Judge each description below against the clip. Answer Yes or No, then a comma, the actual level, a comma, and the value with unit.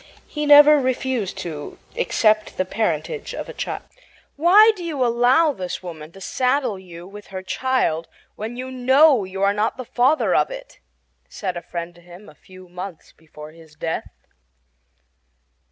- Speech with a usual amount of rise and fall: No, wide, 6.9 semitones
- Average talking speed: Yes, average, 165 wpm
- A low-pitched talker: No, high, 215 Hz